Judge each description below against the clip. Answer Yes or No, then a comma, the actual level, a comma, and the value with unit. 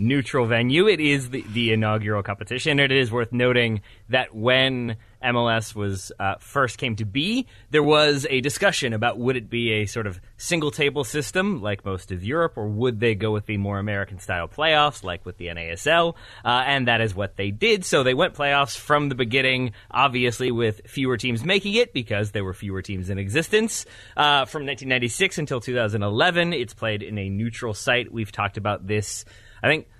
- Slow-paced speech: No, average, 195 wpm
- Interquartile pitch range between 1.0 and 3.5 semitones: No, average, 5.0 semitones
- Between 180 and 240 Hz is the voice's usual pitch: No, low, 120 Hz